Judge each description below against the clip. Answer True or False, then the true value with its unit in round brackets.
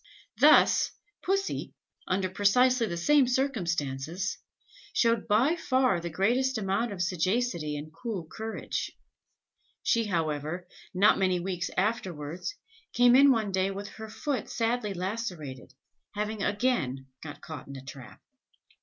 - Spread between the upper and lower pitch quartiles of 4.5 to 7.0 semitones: True (5.6 semitones)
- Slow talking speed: True (125 wpm)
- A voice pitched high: True (195 Hz)